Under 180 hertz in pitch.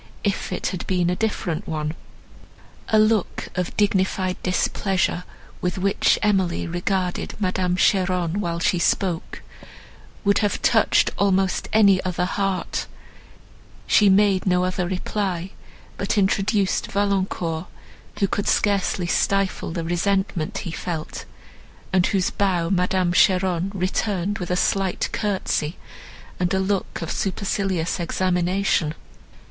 No: medium, 185 Hz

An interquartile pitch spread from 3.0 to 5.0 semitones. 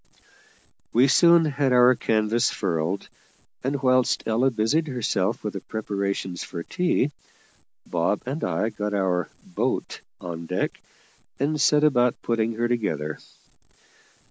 No: wide, 5.4 semitones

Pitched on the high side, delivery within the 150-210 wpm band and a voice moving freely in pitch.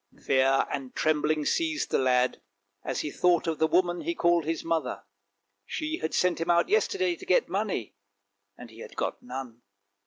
No: medium, 165 Hz; average, 180 wpm; wide, 7.0 semitones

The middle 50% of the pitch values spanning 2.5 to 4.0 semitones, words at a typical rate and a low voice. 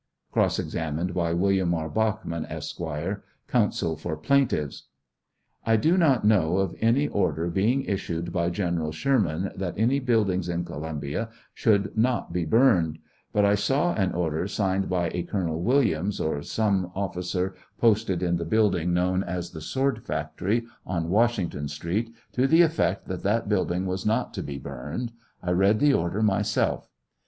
No: average, 4.4 semitones; average, 160 wpm; very low, 95 Hz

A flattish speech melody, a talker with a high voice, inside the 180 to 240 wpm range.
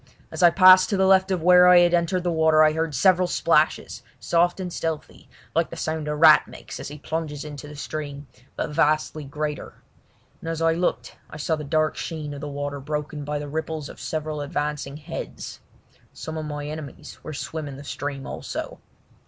No: narrow, 2.1 semitones; medium, 155 Hz; average, 200 wpm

